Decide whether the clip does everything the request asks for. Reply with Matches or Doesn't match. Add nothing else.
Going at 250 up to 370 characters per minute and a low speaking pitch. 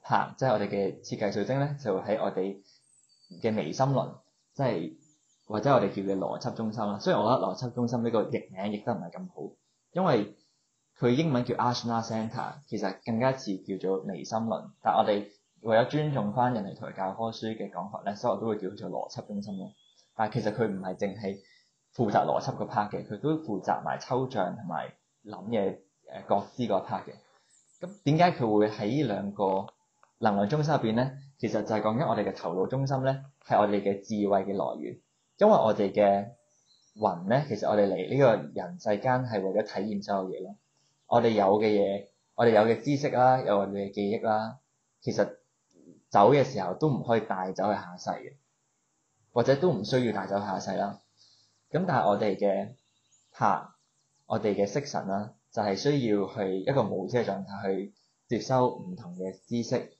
Matches